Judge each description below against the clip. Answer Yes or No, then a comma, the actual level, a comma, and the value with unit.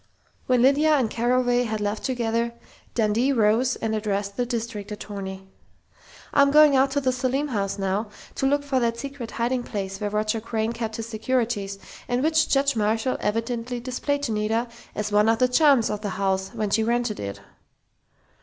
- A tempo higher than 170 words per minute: Yes, average, 180 wpm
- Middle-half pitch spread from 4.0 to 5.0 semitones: No, average, 3.3 semitones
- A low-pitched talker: No, high, 230 Hz